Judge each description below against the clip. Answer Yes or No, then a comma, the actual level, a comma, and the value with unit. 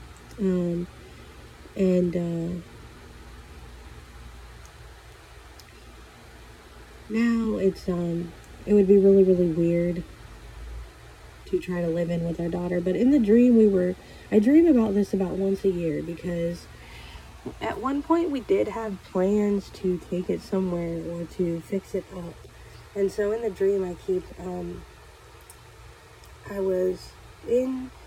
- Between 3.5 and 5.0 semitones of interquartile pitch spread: No, average, 3.0 semitones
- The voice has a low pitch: No, medium, 180 Hz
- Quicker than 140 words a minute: No, slow, 135 wpm